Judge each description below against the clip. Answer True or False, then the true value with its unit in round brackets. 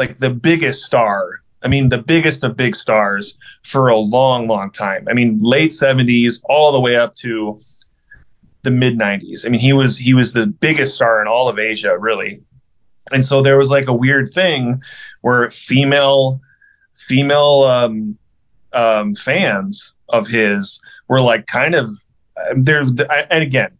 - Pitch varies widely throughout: False (3.3 semitones)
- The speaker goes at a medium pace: True (165 wpm)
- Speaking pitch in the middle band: False (130 Hz)